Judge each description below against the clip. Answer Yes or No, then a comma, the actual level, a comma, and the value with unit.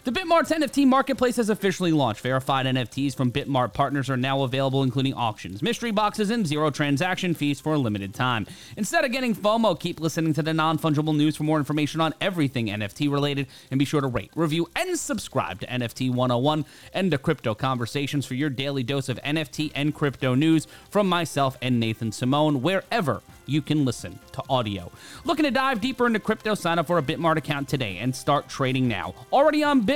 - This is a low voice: No, medium, 150 Hz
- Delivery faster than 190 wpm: Yes, average, 200 wpm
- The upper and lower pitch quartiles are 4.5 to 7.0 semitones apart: Yes, average, 5.1 semitones